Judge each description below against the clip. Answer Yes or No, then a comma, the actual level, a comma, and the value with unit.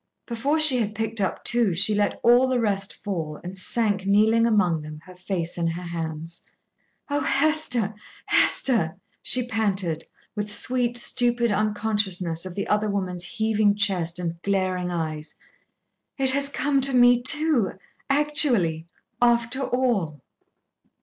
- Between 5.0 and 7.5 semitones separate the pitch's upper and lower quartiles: Yes, average, 5.3 semitones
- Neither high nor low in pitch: No, high, 210 Hz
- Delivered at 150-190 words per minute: No, average, 140 wpm